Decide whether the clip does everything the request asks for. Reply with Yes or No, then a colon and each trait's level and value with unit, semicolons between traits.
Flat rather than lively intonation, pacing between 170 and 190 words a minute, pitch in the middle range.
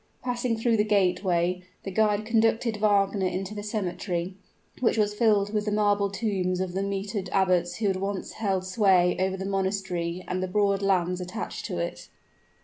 No: narrow, 2.2 semitones; average, 175 wpm; high, 195 Hz